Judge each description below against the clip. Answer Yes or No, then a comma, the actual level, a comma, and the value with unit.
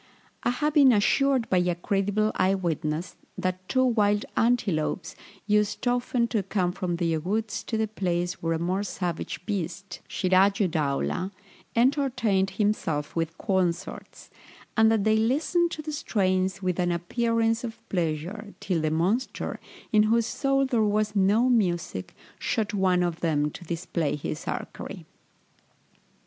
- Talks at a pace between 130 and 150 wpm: Yes, average, 145 wpm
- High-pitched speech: Yes, high, 195 Hz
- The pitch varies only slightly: No, average, 4.3 semitones